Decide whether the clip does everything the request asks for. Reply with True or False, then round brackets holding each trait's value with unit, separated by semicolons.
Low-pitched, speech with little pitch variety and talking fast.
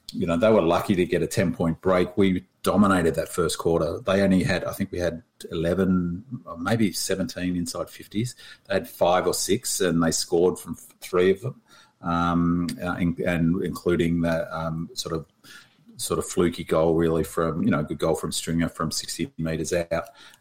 False (85 Hz; 1.7 semitones; 190 wpm)